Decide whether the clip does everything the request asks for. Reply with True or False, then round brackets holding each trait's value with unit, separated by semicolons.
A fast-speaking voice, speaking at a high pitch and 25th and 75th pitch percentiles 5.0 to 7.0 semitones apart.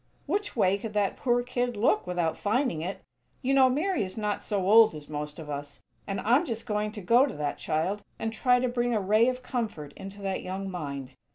True (220 wpm; 210 Hz; 5.3 semitones)